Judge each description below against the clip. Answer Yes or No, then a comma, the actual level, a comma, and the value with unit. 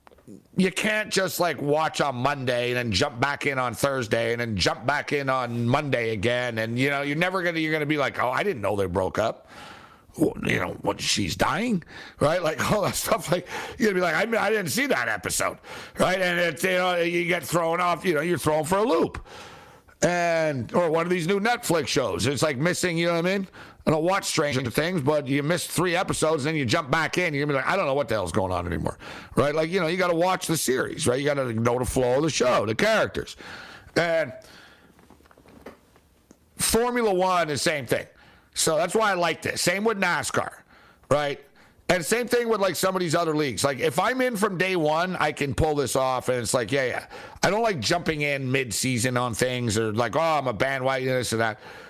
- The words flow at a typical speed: No, fast, 235 wpm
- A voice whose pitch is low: No, medium, 160 Hz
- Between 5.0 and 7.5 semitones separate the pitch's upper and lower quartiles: Yes, wide, 5.6 semitones